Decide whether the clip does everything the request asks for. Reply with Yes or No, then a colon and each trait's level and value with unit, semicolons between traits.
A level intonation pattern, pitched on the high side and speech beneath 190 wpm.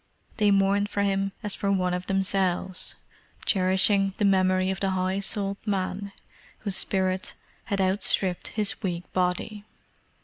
Yes: narrow, 1.2 semitones; high, 195 Hz; average, 140 wpm